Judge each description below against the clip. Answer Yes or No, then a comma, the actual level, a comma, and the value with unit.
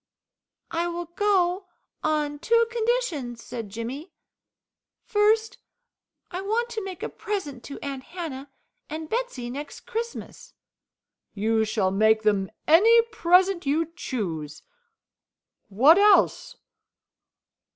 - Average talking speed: No, slow, 110 wpm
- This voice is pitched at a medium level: No, very high, 330 Hz